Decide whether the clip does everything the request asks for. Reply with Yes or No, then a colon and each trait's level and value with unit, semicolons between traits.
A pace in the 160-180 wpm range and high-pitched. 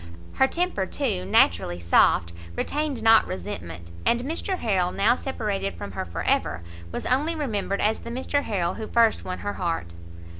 Yes: average, 165 wpm; high, 205 Hz